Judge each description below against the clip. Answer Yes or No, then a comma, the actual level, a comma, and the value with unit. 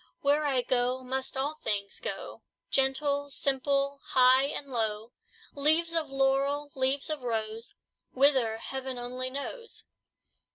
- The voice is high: Yes, very high, 270 Hz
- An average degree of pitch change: No, narrow, 2.1 semitones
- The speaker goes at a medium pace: No, slow, 125 wpm